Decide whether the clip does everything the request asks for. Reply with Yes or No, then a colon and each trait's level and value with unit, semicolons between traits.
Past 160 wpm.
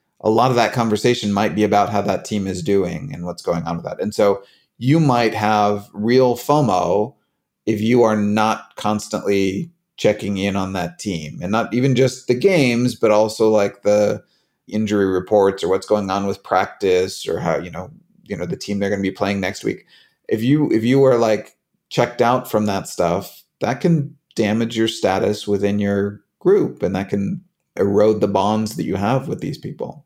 Yes: average, 200 wpm